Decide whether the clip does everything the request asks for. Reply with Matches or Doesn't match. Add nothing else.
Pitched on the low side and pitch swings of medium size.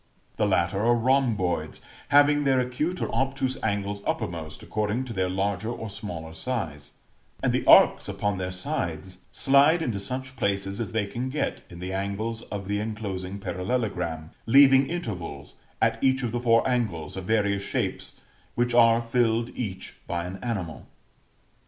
Matches